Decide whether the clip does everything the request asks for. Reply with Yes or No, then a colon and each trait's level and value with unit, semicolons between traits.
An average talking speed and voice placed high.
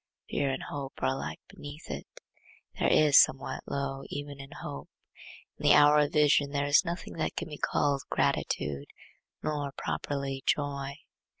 No: average, 160 wpm; medium, 140 Hz